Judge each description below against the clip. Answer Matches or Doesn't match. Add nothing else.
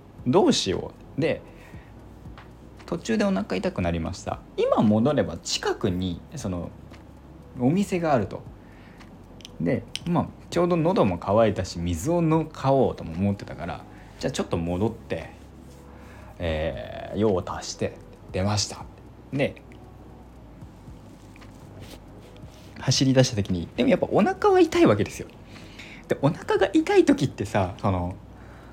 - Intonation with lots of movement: Matches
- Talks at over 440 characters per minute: Doesn't match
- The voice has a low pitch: Matches